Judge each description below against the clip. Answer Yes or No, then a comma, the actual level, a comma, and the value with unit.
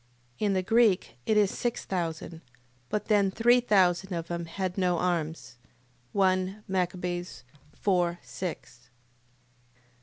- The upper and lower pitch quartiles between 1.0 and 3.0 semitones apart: Yes, narrow, 2.5 semitones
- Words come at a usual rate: No, slow, 120 wpm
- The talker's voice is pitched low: No, medium, 185 Hz